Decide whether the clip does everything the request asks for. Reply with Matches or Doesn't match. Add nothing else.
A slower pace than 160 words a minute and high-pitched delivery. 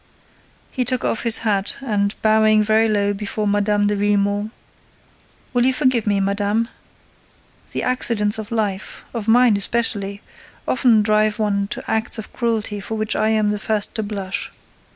Matches